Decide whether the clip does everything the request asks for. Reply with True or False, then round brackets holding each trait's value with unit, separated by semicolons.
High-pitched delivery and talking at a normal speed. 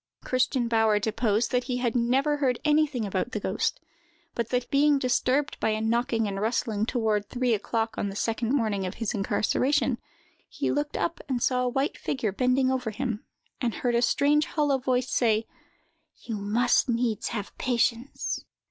True (240 Hz; 175 wpm)